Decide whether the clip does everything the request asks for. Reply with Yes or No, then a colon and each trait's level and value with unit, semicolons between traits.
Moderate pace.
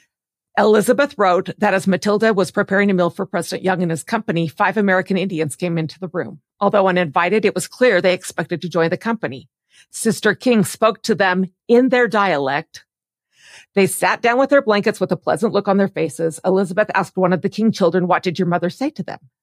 No: fast, 210 wpm